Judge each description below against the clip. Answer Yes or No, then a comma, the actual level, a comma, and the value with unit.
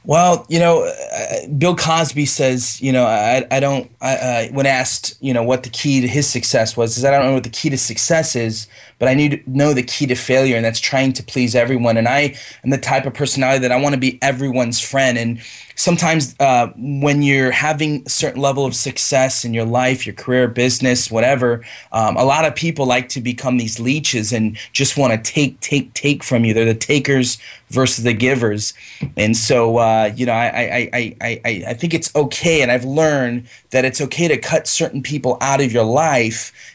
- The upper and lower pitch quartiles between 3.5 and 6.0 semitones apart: No, average, 3.0 semitones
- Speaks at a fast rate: Yes, fast, 220 wpm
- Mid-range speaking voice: No, low, 130 Hz